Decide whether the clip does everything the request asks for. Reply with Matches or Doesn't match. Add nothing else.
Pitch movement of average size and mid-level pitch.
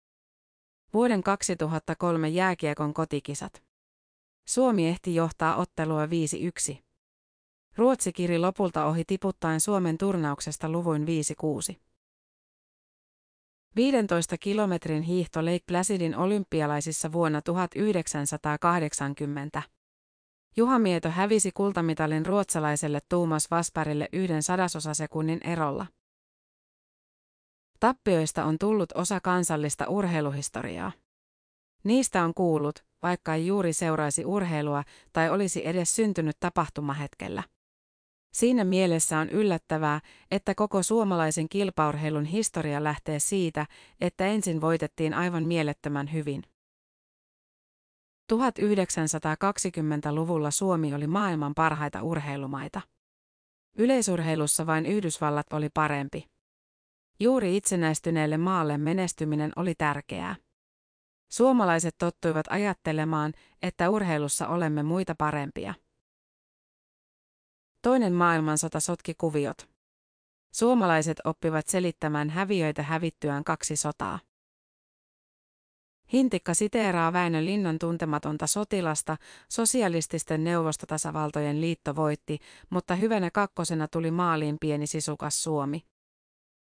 Matches